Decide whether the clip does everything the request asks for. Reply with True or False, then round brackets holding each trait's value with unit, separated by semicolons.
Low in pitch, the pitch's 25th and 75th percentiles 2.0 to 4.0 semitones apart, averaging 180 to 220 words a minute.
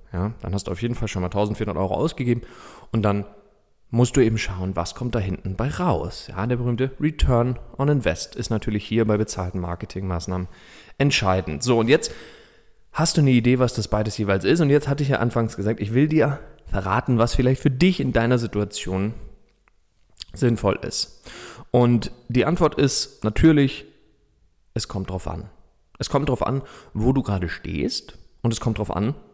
False (115 Hz; 4.5 semitones; 185 wpm)